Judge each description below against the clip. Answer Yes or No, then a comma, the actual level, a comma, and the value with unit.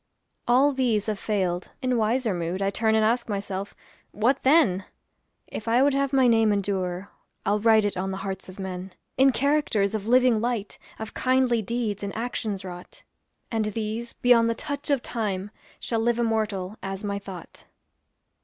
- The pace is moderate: Yes, average, 175 wpm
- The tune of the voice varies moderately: Yes, average, 3.6 semitones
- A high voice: Yes, high, 220 Hz